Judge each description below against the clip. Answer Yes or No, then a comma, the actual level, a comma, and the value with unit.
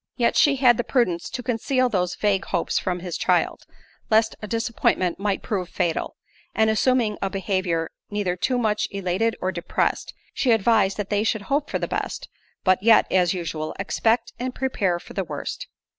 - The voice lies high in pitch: Yes, high, 205 Hz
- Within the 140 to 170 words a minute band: No, average, 180 wpm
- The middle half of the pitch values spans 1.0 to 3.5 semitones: No, average, 4.0 semitones